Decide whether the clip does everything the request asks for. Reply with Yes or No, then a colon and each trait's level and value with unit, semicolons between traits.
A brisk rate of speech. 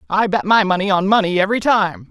Yes: fast, 230 wpm